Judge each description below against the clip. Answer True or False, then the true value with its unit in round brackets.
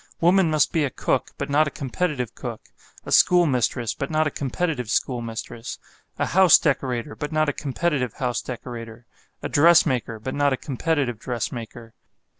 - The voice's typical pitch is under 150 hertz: True (135 Hz)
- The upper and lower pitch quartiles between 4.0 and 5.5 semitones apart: True (4.3 semitones)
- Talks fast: False (165 wpm)